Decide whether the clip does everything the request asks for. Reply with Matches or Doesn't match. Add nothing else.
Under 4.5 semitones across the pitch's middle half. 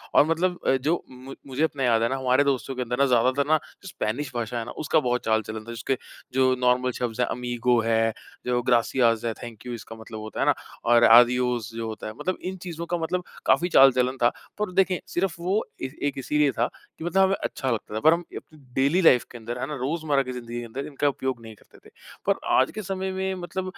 Doesn't match